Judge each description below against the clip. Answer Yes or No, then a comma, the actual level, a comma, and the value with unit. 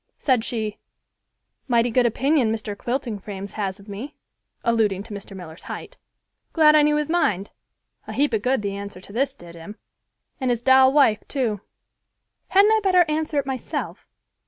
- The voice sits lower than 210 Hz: No, high, 235 Hz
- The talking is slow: No, average, 175 wpm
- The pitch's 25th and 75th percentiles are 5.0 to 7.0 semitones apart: Yes, wide, 5.5 semitones